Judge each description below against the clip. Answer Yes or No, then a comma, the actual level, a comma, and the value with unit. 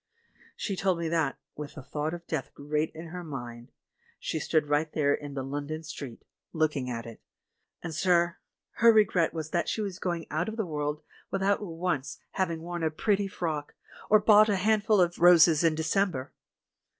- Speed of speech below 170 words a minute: No, average, 195 wpm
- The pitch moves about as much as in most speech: Yes, average, 3.9 semitones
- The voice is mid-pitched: Yes, medium, 165 Hz